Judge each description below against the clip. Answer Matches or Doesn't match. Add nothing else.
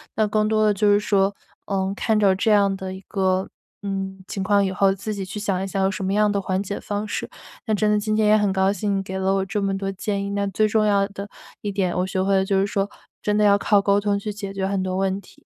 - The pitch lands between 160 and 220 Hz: Matches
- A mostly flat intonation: Matches